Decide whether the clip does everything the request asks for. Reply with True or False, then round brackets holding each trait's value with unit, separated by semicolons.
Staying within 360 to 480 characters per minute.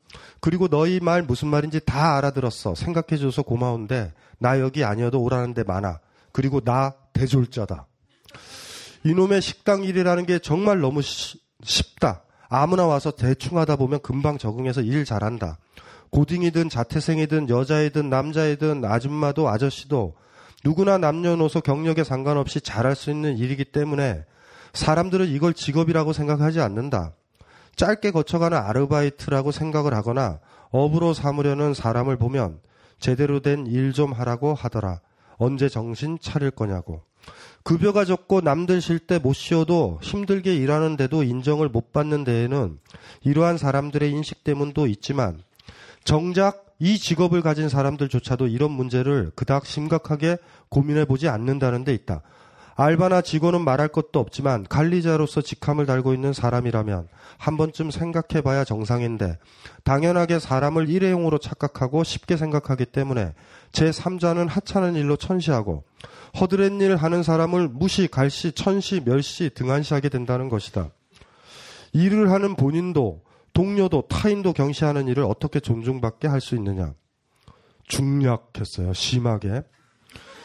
False (325 characters per minute)